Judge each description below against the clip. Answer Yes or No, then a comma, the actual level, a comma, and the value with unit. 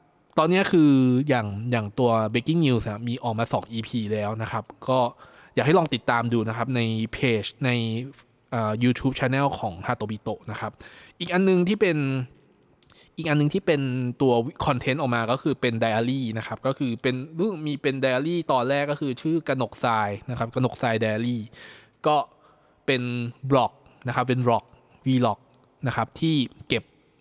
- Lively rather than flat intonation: No, average, 3.5 semitones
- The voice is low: Yes, low, 125 Hz